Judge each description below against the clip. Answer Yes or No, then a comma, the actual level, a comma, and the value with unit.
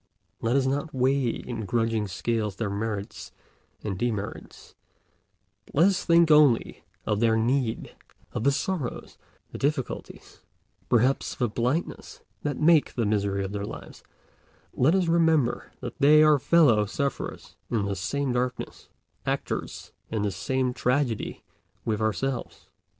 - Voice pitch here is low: Yes, low, 125 Hz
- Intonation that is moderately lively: Yes, average, 4.6 semitones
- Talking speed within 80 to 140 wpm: Yes, slow, 135 wpm